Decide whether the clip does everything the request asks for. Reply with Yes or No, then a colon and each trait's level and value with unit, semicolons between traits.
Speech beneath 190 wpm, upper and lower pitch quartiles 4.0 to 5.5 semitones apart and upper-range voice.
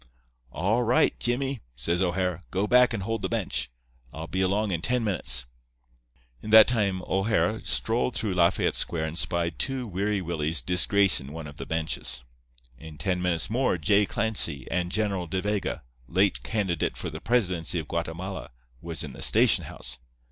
No: average, 170 wpm; average, 4.4 semitones; very low, 95 Hz